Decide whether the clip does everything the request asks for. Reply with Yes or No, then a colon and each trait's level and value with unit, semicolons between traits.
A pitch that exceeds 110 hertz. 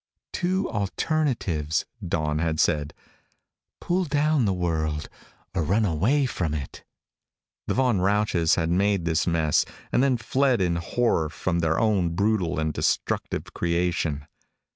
No: very low, 90 Hz